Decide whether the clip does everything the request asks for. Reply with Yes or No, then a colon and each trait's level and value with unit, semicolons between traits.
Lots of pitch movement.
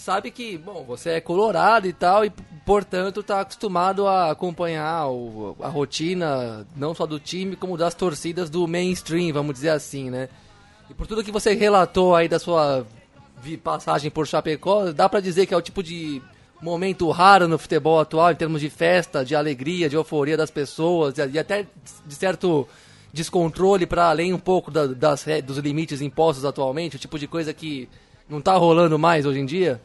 No: average, 3.7 semitones